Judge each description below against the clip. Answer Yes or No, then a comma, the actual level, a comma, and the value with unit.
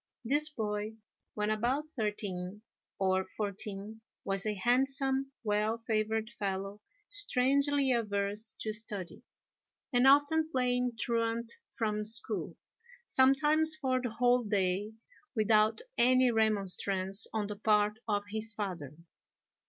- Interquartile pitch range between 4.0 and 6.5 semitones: No, average, 3.4 semitones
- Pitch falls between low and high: No, high, 220 Hz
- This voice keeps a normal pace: No, slow, 115 wpm